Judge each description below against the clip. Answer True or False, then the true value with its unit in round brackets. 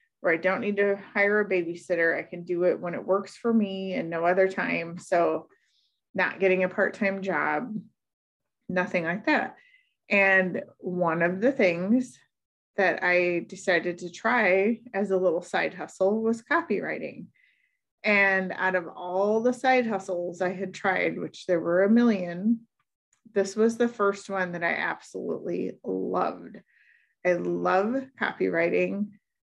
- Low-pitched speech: False (190 Hz)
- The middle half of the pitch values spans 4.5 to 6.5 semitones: False (3.2 semitones)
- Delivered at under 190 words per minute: True (155 wpm)